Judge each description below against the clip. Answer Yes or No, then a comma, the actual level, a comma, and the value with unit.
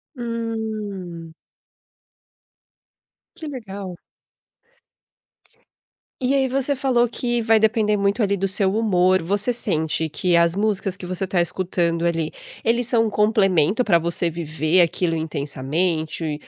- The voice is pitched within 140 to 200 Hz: Yes, high, 190 Hz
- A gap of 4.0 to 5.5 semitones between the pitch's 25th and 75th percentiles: Yes, average, 4.9 semitones